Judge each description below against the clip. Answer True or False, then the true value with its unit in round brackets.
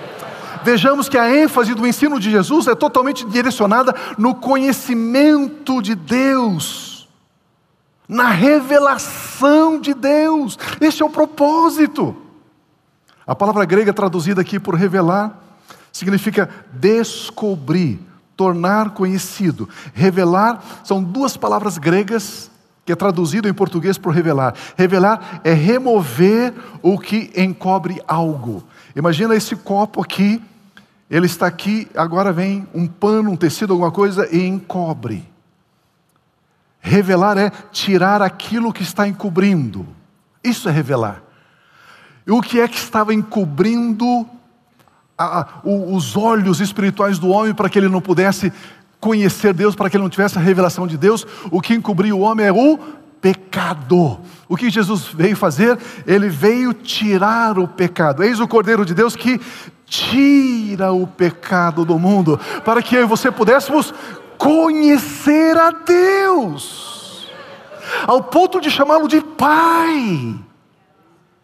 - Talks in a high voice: True (205 Hz)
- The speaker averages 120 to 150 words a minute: True (130 wpm)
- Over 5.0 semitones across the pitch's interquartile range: False (4.7 semitones)